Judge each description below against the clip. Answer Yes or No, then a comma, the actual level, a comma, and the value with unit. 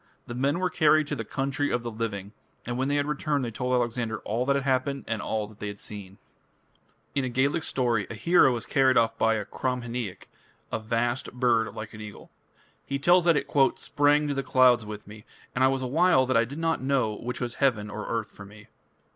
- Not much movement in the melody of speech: No, average, 3.8 semitones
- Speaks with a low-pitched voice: Yes, low, 125 Hz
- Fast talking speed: Yes, fast, 225 wpm